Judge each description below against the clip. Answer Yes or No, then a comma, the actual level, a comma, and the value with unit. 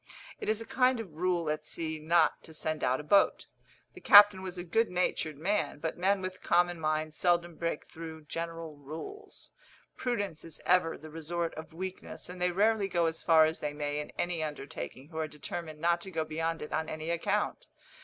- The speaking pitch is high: No, medium, 165 Hz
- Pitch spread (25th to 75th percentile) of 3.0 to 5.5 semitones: No, narrow, 2.5 semitones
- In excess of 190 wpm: Yes, fast, 205 wpm